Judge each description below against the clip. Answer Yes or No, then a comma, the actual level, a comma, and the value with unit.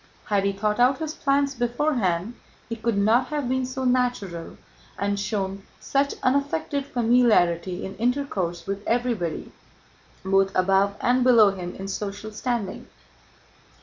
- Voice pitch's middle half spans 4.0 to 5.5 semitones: Yes, average, 4.6 semitones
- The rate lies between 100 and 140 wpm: Yes, slow, 135 wpm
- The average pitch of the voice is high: Yes, high, 225 Hz